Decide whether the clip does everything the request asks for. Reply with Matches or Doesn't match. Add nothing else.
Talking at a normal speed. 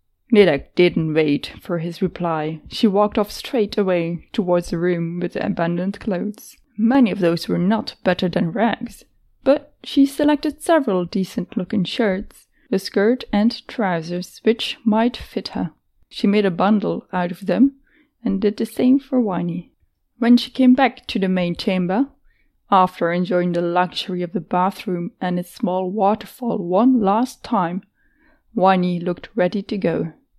Matches